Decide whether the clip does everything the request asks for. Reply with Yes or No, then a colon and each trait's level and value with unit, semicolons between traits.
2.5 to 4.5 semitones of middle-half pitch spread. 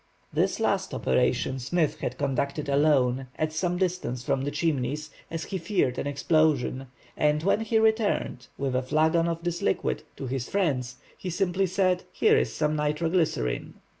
No: average, 4.9 semitones